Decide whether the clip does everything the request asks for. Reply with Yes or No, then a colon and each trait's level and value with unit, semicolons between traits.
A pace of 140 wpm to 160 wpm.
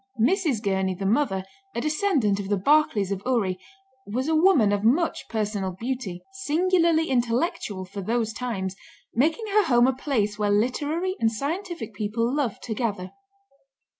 Yes: average, 155 wpm